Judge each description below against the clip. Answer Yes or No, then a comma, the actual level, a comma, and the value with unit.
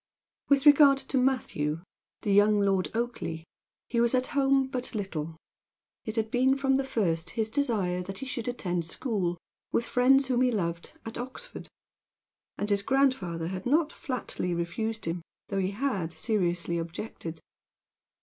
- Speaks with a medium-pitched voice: No, high, 220 Hz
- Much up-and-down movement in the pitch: Yes, wide, 6.6 semitones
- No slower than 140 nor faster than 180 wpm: Yes, average, 155 wpm